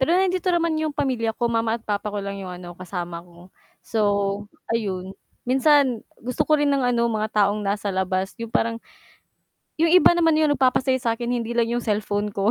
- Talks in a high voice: Yes, high, 230 Hz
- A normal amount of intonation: Yes, average, 4.7 semitones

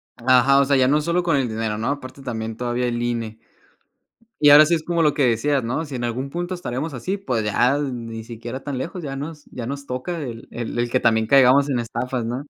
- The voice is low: Yes, low, 130 Hz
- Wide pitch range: No, average, 3.5 semitones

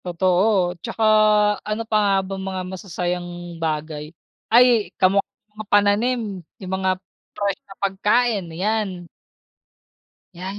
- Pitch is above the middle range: Yes, high, 195 Hz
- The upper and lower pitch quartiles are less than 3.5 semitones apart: Yes, average, 2.8 semitones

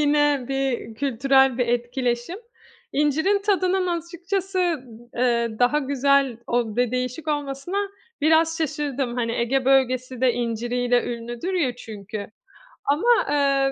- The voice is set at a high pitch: Yes, very high, 270 Hz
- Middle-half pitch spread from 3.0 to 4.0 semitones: Yes, average, 3.7 semitones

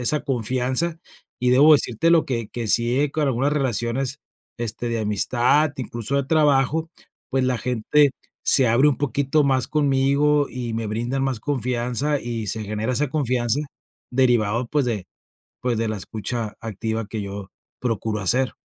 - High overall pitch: No, low, 125 Hz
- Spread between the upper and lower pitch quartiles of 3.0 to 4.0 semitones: Yes, average, 3.5 semitones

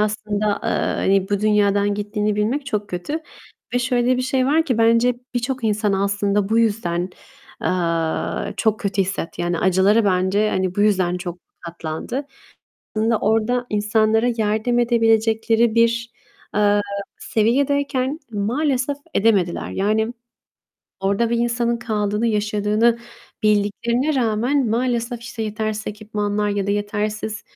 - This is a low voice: No, high, 215 Hz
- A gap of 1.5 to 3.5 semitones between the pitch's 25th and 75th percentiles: Yes, narrow, 2.6 semitones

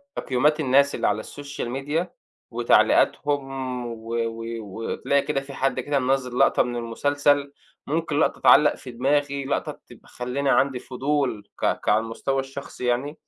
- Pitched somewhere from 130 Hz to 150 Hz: Yes, low, 135 Hz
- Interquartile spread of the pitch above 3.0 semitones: No, average, 2.7 semitones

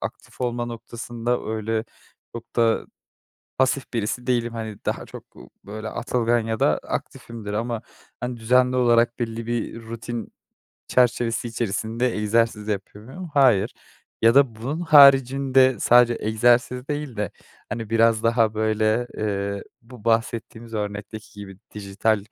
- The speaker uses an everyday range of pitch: No, narrow, 2.0 semitones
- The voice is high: No, low, 115 Hz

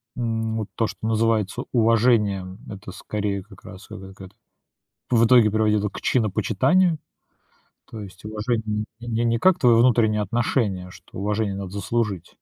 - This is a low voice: Yes, low, 110 Hz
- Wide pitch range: No, narrow, 2.6 semitones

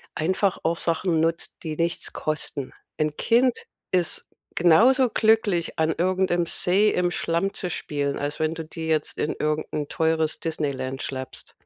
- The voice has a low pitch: No, medium, 165 Hz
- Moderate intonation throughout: Yes, average, 3.0 semitones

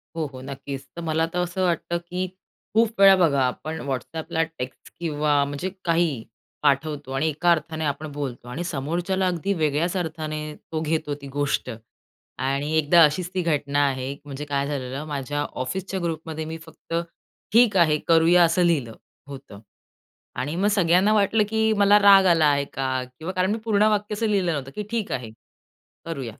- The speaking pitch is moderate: Yes, medium, 160 Hz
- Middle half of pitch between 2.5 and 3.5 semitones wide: No, average, 4.1 semitones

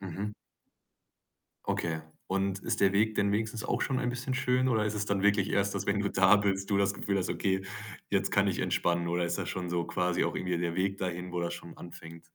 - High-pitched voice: No, very low, 95 Hz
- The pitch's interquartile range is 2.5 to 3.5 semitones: Yes, average, 2.8 semitones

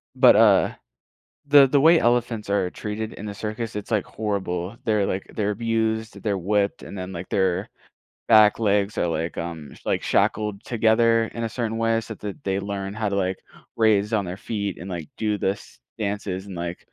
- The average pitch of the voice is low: Yes, low, 105 Hz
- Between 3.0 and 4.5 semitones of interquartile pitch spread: No, narrow, 2.5 semitones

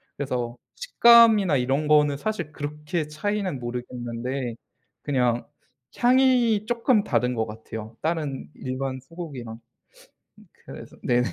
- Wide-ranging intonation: Yes, wide, 7.8 semitones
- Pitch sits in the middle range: Yes, medium, 145 Hz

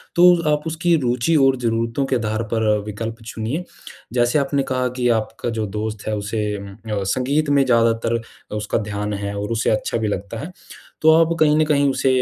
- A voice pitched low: Yes, low, 115 Hz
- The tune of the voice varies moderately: Yes, average, 4.6 semitones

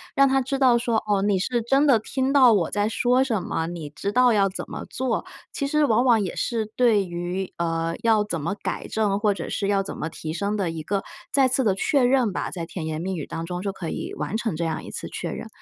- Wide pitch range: Yes, wide, 5.8 semitones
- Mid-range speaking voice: No, high, 205 Hz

